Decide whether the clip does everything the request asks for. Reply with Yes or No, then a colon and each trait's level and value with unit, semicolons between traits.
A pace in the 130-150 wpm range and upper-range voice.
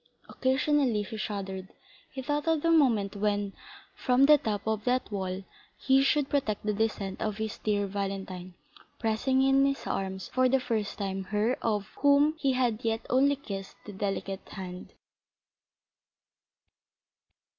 Yes: average, 145 wpm; high, 220 Hz